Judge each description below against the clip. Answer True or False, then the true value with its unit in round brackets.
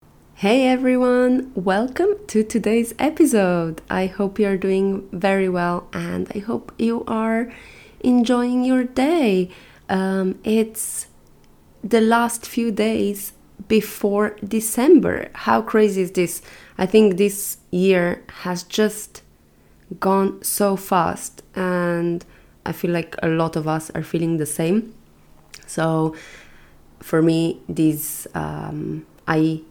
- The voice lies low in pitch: False (195 Hz)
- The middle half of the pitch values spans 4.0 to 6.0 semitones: True (5.2 semitones)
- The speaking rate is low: True (120 wpm)